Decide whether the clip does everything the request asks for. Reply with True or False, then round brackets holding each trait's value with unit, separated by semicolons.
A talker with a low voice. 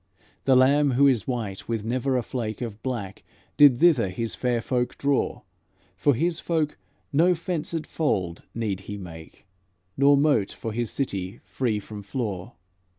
True (120 Hz)